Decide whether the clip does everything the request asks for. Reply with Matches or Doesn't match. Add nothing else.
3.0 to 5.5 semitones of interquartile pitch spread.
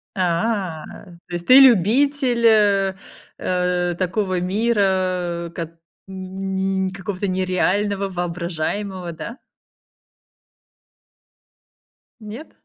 Doesn't match